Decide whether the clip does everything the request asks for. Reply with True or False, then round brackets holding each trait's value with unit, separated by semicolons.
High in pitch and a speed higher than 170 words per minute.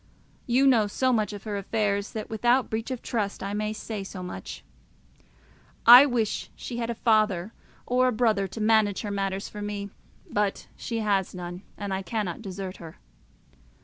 True (210 Hz; 180 wpm)